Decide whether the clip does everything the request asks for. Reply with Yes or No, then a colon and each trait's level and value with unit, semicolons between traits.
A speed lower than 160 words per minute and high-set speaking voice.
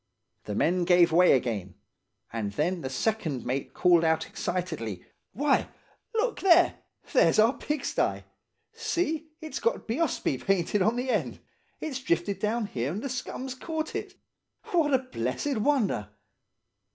Yes: average, 140 wpm; high, 210 Hz